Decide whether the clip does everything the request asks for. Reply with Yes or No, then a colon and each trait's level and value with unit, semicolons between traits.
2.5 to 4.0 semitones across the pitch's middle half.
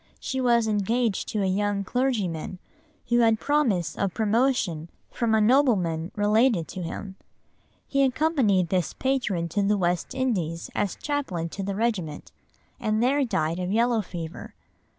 No: average, 5.2 semitones